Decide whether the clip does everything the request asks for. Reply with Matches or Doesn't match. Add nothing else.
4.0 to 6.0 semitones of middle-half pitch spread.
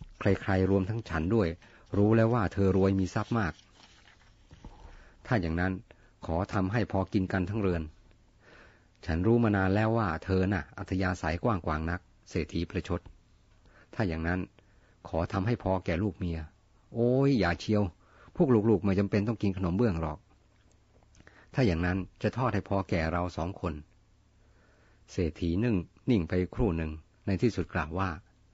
Doesn't match